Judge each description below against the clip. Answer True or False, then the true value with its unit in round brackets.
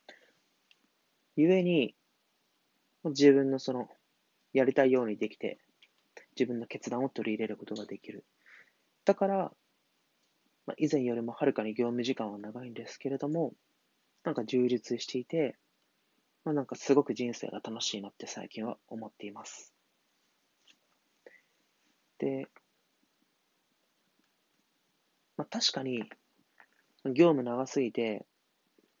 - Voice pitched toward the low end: True (125 Hz)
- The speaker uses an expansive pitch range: False (3.4 semitones)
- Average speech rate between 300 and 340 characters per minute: False (215 characters per minute)